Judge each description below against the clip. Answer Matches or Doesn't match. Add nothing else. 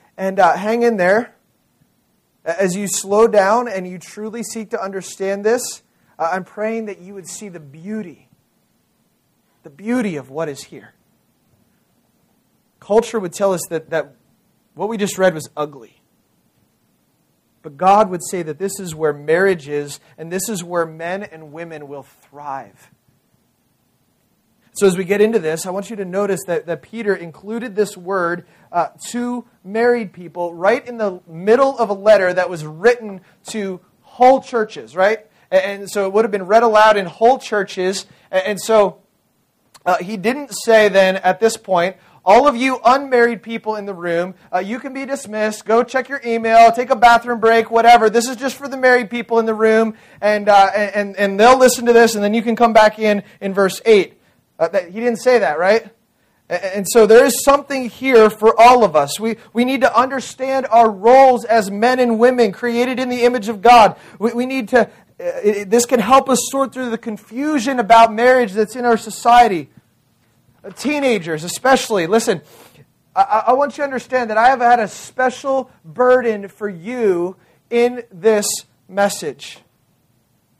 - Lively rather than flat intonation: Doesn't match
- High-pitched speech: Matches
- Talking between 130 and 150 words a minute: Doesn't match